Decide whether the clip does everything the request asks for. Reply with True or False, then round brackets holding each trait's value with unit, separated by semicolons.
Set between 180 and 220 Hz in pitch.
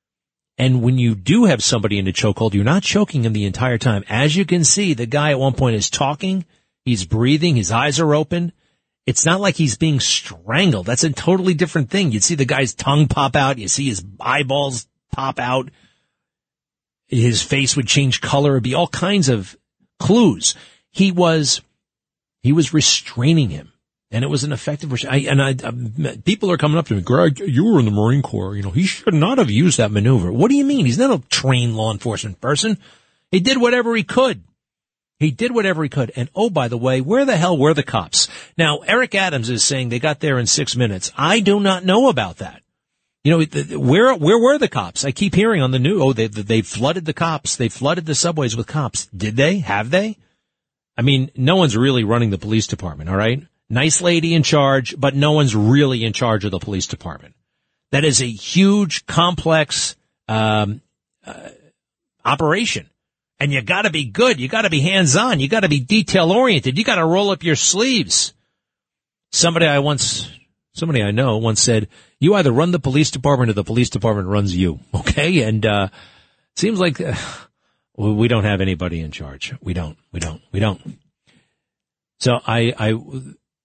False (135 Hz)